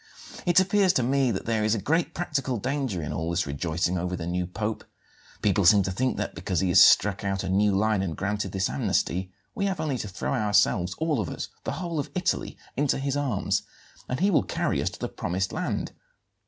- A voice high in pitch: No, low, 105 Hz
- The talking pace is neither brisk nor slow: No, fast, 220 wpm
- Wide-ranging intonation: Yes, wide, 6.9 semitones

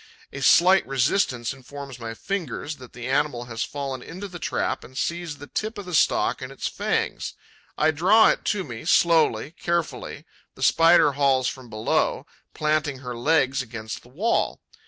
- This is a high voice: No, medium, 145 Hz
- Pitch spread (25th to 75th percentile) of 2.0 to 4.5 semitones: No, average, 5.2 semitones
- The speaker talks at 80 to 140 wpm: No, average, 170 wpm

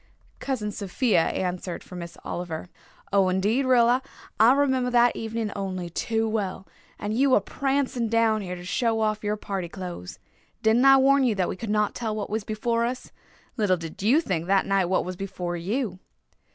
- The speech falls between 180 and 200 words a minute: Yes, average, 185 wpm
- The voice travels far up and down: No, average, 4.4 semitones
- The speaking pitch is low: No, high, 210 Hz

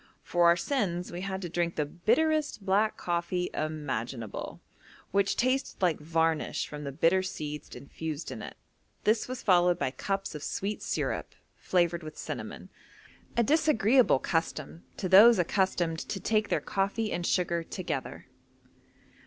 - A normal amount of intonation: Yes, average, 4.2 semitones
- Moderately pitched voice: Yes, medium, 180 Hz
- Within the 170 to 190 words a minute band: No, average, 145 wpm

